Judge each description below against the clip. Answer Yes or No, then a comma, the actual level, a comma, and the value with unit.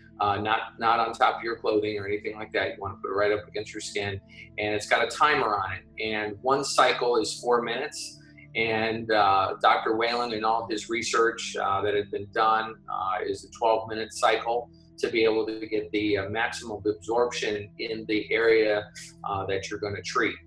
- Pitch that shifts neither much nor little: No, narrow, 1.4 semitones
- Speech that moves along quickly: Yes, fast, 215 wpm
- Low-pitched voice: Yes, low, 110 Hz